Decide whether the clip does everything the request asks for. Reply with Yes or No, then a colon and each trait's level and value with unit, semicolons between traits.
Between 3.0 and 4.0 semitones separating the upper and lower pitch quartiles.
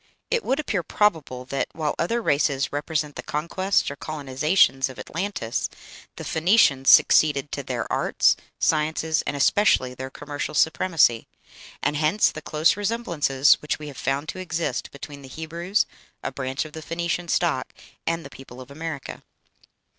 Yes: average, 3.6 semitones